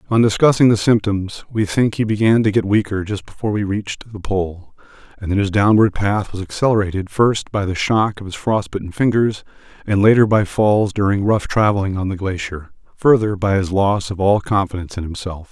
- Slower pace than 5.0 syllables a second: No, 5.4 syllables/s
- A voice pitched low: Yes, low, 100 Hz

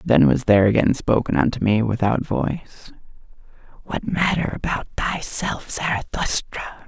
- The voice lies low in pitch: Yes, low, 120 Hz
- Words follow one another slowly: Yes, slow, 120 wpm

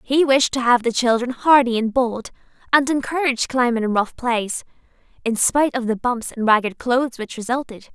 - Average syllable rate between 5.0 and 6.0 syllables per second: Yes, 5.3 syllables/s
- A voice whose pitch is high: Yes, high, 245 Hz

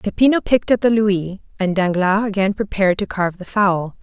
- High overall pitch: Yes, high, 200 Hz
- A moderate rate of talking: Yes, average, 195 wpm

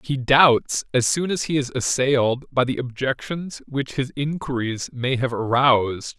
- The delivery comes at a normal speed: Yes, average, 165 wpm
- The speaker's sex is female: No, male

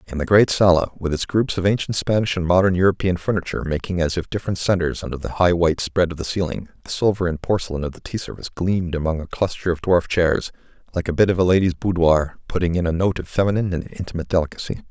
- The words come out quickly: Yes, fast, 235 wpm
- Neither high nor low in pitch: No, very low, 90 Hz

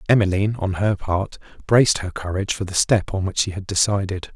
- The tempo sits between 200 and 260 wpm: Yes, fast, 205 wpm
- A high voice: No, very low, 95 Hz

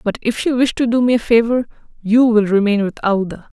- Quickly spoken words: Yes, fast, 235 wpm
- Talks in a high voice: Yes, high, 225 Hz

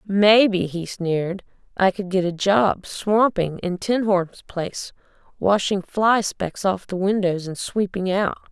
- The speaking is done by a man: No, female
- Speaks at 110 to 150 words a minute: Yes, average, 140 wpm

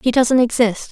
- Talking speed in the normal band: Yes, average, 195 wpm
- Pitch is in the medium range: No, high, 240 Hz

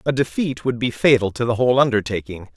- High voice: No, low, 120 Hz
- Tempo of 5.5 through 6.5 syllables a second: Yes, 6.3 syllables/s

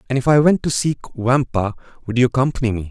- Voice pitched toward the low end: Yes, low, 125 Hz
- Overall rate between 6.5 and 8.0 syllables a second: Yes, 6.8 syllables/s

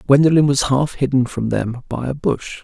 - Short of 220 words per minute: Yes, fast, 205 wpm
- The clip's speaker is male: Yes, male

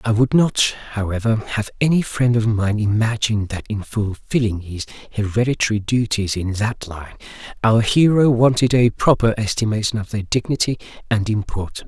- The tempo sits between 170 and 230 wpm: No, average, 150 wpm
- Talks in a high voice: No, low, 110 Hz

